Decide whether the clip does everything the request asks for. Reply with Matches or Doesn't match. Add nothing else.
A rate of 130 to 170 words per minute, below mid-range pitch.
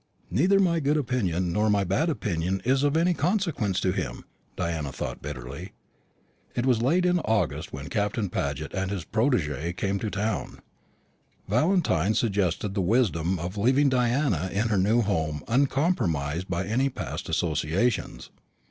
Matches